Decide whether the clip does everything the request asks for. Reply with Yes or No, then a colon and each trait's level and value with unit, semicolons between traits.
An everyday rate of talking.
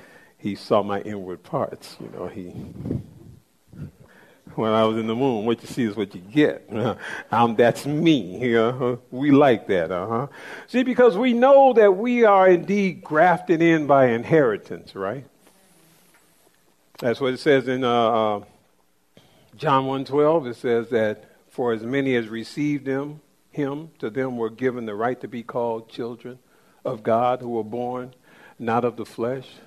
Yes: average, 165 wpm